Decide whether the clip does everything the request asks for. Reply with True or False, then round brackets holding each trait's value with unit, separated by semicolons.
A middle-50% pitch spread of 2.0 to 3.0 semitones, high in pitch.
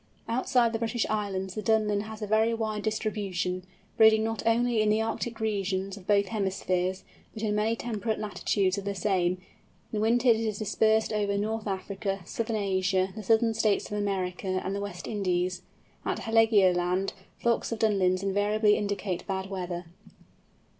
True (2.5 semitones; 210 Hz)